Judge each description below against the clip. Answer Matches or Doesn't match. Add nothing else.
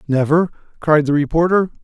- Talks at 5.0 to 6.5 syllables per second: Matches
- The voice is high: Doesn't match